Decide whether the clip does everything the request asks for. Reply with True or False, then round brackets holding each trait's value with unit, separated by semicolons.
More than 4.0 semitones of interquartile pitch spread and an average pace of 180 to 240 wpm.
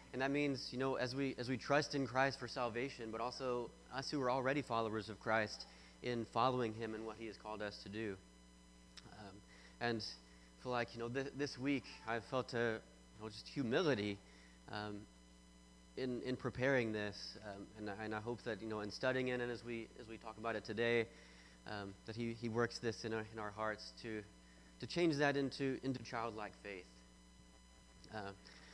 True (5.2 semitones; 200 wpm)